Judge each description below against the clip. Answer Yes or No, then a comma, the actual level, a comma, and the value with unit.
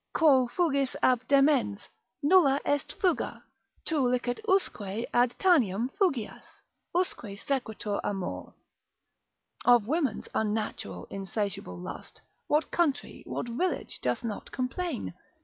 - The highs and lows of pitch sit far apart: Yes, wide, 6.1 semitones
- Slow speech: Yes, slow, 110 wpm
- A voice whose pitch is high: Yes, very high, 250 Hz